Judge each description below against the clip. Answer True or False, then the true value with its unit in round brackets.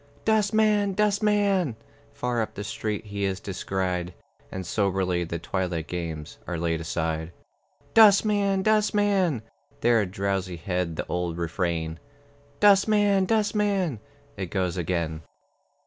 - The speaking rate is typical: False (110 wpm)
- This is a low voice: True (100 Hz)